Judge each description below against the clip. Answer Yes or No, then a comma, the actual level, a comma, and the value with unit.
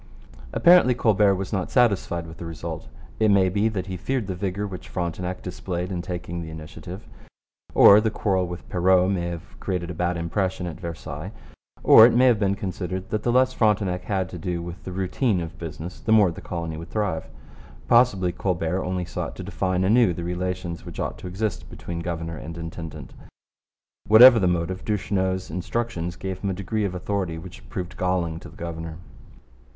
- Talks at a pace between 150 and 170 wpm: No, average, 190 wpm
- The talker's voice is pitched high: No, very low, 90 Hz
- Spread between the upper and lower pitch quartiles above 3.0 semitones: No, average, 2.7 semitones